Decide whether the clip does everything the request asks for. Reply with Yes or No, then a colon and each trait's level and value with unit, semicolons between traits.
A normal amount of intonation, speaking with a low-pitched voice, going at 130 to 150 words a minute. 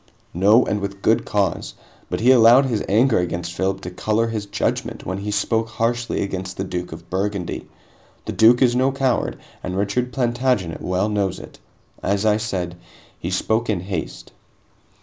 No: average, 3.8 semitones; low, 105 Hz; average, 170 wpm